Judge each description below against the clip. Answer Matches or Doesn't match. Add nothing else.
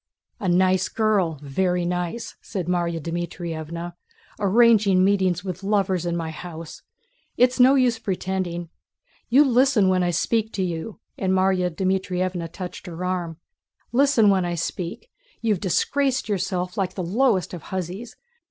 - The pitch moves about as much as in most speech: Matches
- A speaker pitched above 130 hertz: Matches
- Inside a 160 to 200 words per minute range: Doesn't match